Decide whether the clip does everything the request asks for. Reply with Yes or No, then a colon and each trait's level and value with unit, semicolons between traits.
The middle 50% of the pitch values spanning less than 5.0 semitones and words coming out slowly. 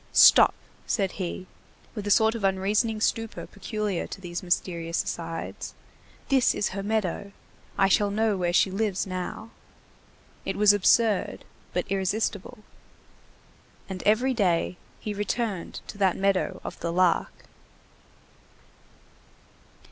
Yes: narrow, 2.6 semitones; slow, 125 wpm